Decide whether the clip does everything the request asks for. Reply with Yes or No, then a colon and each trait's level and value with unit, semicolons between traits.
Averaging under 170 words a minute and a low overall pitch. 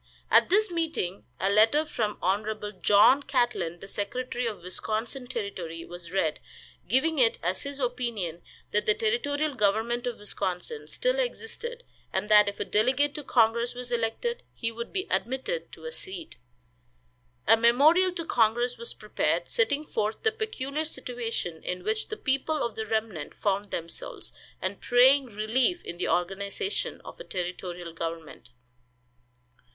No: average, 150 wpm; high, 235 Hz